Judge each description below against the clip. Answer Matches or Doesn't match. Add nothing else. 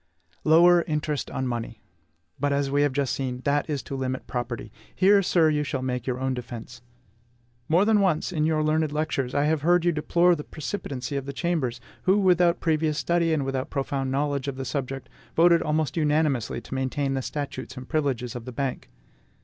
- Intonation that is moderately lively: Matches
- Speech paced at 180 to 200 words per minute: Matches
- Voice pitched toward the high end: Doesn't match